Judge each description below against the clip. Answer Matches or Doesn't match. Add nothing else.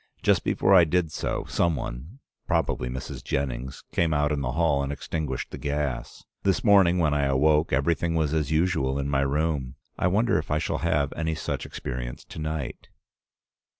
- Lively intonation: Doesn't match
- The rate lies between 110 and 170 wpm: Doesn't match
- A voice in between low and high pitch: Doesn't match